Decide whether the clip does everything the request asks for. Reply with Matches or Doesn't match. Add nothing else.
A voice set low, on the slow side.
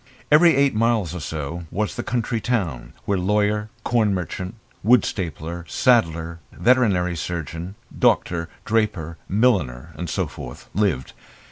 Matches